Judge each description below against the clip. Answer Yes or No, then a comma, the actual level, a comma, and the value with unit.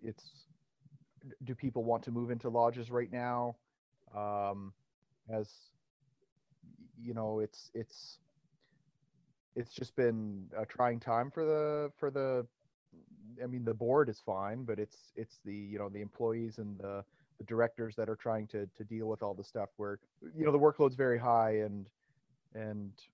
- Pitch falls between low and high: No, low, 120 Hz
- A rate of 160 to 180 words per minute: Yes, average, 165 wpm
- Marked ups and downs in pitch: No, average, 4.2 semitones